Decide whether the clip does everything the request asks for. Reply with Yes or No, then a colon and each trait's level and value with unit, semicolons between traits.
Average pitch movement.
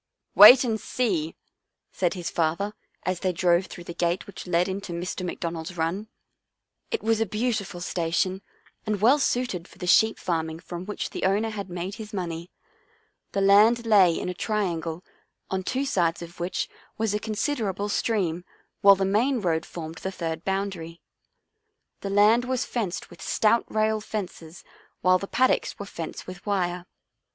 Yes: average, 3.7 semitones